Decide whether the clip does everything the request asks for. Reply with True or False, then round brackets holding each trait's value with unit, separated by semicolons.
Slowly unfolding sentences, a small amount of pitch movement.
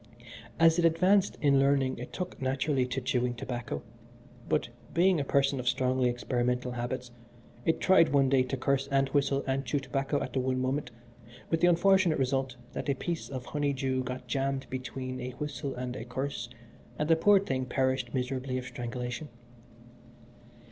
False (170 wpm; 2.1 semitones)